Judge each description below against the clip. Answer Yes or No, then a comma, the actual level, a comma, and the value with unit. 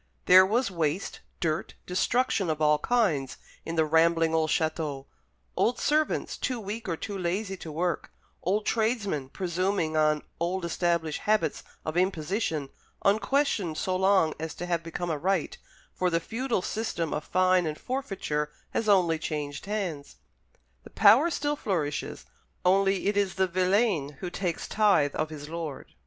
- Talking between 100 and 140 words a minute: No, average, 155 wpm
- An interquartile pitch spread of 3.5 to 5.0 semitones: Yes, average, 4.2 semitones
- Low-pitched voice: No, medium, 175 Hz